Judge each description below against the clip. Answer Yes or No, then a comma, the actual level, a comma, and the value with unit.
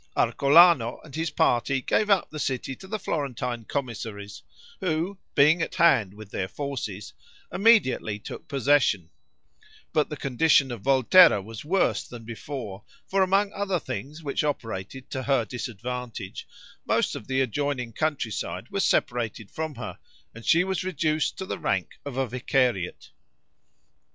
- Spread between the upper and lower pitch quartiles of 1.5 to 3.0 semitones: No, wide, 5.5 semitones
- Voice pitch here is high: No, low, 135 Hz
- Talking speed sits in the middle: Yes, average, 145 wpm